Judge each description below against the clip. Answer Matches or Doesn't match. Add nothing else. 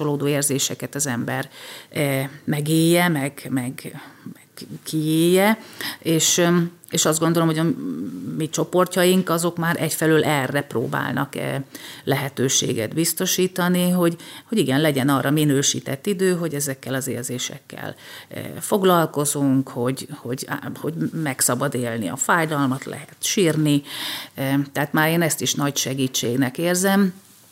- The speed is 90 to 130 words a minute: Matches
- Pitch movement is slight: Doesn't match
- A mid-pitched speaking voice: Matches